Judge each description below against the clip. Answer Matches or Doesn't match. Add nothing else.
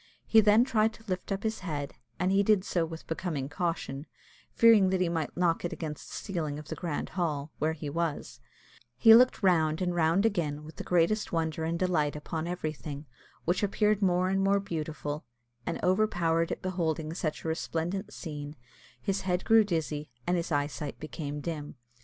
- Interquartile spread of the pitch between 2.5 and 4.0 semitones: Matches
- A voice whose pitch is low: Doesn't match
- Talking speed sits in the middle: Matches